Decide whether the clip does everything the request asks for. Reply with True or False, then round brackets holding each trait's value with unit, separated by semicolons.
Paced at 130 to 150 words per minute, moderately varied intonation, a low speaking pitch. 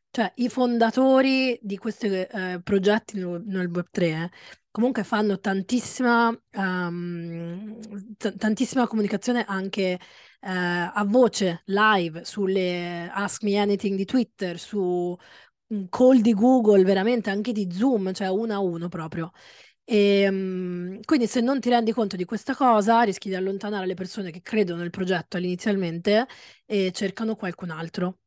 False (140 wpm; 3.6 semitones; 200 Hz)